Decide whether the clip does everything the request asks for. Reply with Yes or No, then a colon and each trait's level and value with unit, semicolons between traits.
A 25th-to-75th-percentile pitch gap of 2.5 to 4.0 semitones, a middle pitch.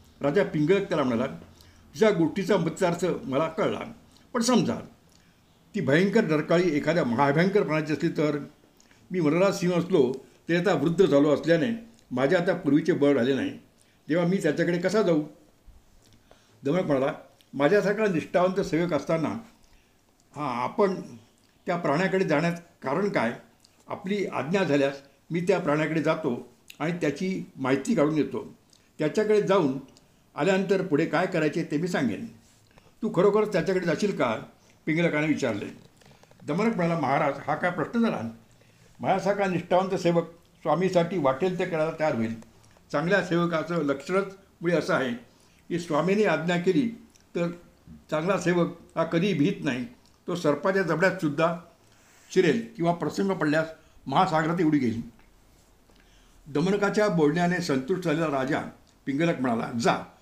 No: average, 4.6 semitones; medium, 165 Hz